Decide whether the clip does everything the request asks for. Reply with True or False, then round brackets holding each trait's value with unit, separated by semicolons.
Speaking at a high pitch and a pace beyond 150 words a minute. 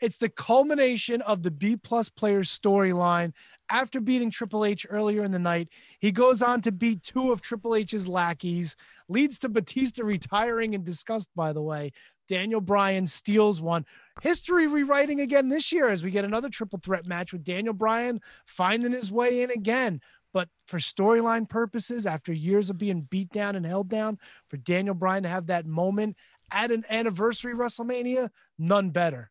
True (210 Hz; 175 wpm)